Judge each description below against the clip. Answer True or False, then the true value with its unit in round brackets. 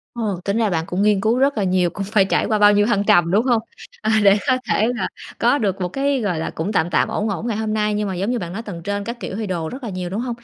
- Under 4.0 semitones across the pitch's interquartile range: True (3.2 semitones)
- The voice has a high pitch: True (205 Hz)